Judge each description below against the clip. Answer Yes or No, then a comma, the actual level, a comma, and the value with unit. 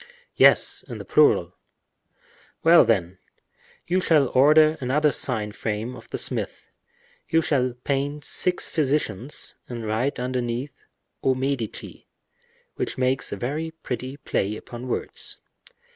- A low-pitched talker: Yes, low, 130 Hz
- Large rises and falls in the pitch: No, average, 3.8 semitones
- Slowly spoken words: Yes, slow, 125 wpm